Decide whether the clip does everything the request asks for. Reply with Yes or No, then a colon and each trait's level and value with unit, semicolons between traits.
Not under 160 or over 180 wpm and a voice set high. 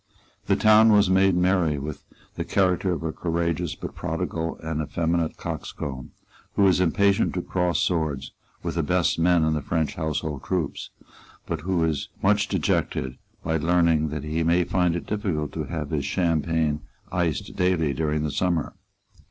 No: average, 165 wpm; very low, 80 Hz